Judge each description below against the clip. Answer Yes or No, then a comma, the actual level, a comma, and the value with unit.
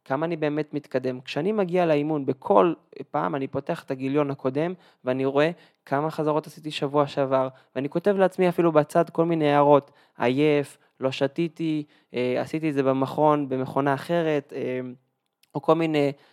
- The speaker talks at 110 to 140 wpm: No, fast, 150 wpm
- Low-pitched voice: No, medium, 145 Hz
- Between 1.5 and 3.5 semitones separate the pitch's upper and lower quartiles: Yes, average, 2.7 semitones